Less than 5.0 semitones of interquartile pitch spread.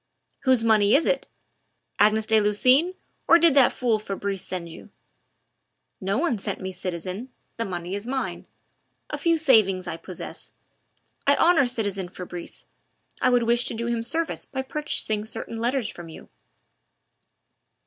No: average, 5.3 semitones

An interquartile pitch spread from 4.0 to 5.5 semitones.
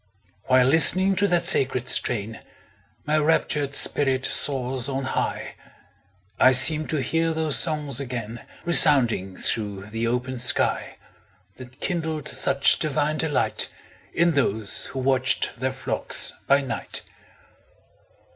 No: average, 3.6 semitones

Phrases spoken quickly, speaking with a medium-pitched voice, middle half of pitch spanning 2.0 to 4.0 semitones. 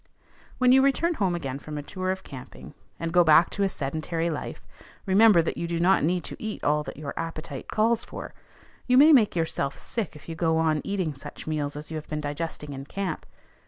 No: fast, 220 wpm; medium, 165 Hz; average, 4.6 semitones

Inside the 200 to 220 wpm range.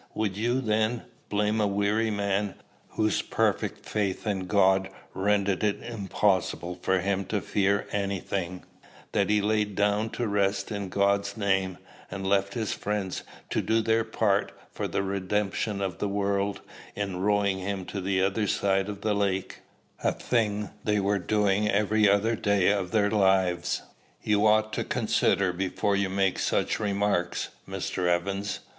No: average, 160 wpm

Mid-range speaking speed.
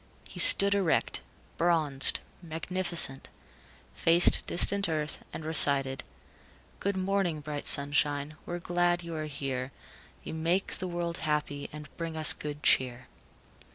No: slow, 125 wpm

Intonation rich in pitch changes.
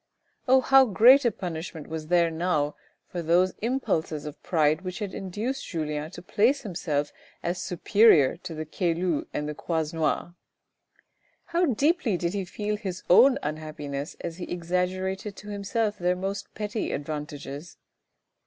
No: average, 4.8 semitones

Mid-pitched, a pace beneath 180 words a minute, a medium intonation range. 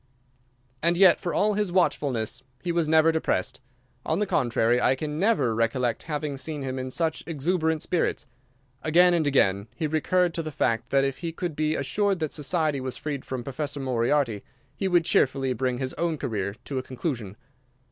No: medium, 150 Hz; average, 185 wpm; average, 4.5 semitones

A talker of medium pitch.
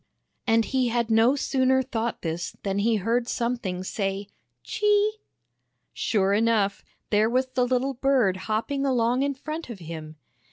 No: high, 235 Hz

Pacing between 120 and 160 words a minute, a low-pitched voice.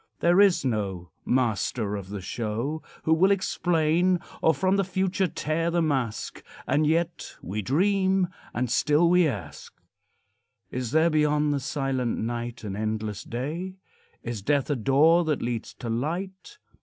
No: average, 150 wpm; medium, 150 Hz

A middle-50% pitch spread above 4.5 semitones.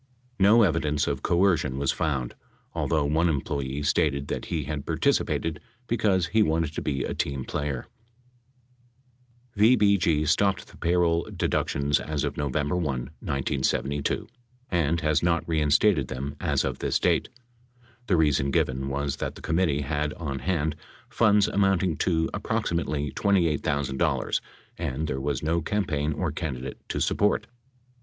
No: average, 3.6 semitones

